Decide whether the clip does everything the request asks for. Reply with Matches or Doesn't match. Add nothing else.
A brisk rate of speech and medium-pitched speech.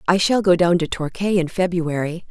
Matches